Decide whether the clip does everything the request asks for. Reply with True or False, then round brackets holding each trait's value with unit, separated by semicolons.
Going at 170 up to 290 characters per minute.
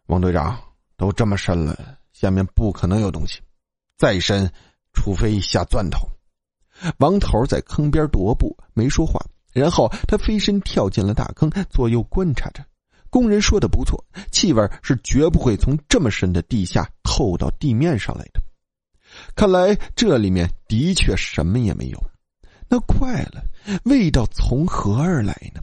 True (225 characters per minute)